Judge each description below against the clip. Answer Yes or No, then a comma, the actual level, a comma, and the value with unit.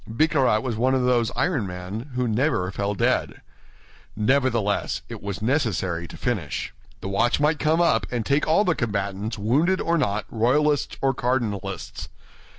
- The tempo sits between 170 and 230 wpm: No, average, 155 wpm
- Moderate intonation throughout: No, wide, 5.8 semitones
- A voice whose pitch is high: No, low, 120 Hz